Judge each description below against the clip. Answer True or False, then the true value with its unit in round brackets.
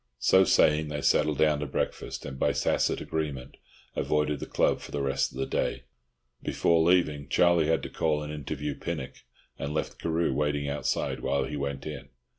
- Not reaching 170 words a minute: False (185 wpm)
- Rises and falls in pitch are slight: True (1.9 semitones)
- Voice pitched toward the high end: False (75 Hz)